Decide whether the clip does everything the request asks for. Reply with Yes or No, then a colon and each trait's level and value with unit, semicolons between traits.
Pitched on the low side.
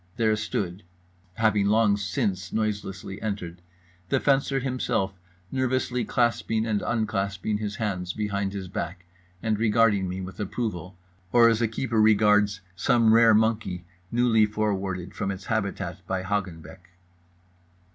Yes: low, 105 Hz